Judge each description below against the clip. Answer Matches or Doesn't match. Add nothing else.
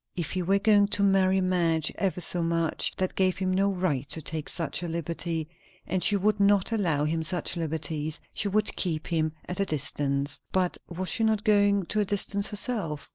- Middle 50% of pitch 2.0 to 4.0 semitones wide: Matches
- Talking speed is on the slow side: Doesn't match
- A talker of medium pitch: Matches